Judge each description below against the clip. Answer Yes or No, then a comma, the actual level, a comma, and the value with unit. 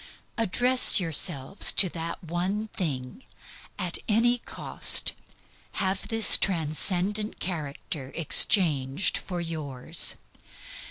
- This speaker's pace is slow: Yes, slow, 90 wpm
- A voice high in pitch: No, medium, 175 Hz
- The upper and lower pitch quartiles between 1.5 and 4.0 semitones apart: No, average, 4.9 semitones